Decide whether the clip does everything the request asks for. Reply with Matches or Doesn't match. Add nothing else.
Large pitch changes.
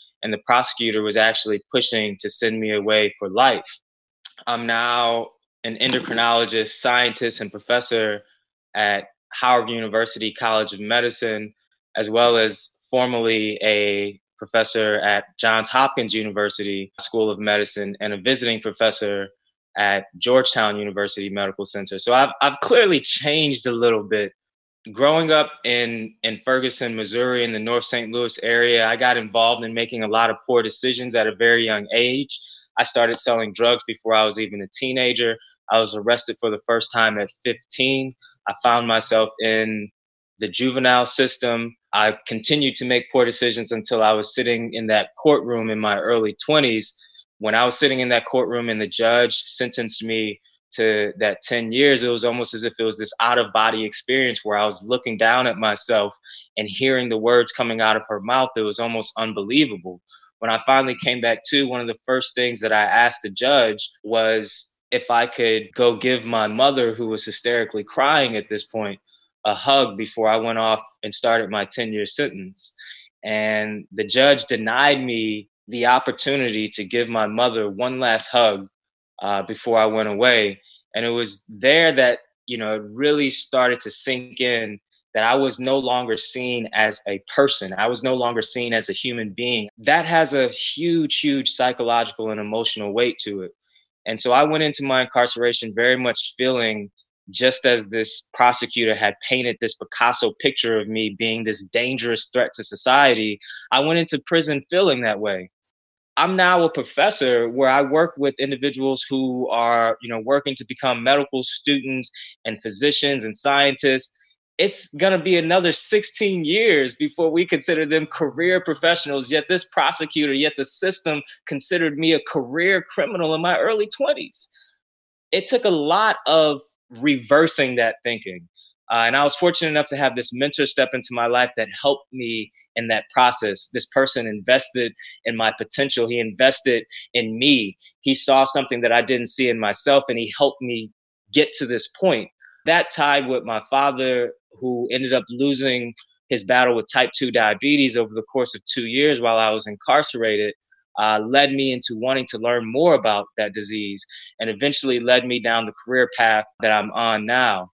Doesn't match